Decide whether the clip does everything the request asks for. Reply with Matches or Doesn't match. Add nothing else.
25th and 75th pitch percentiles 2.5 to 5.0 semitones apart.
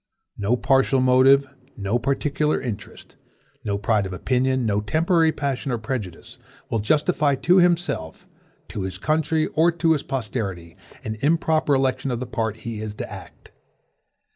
Doesn't match